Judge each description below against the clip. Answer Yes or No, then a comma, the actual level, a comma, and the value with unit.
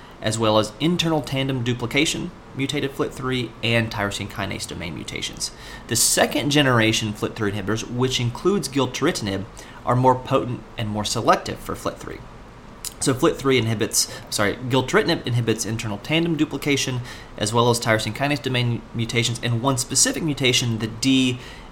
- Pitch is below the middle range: Yes, low, 120 Hz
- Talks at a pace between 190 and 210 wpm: No, average, 140 wpm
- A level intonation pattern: No, average, 3.2 semitones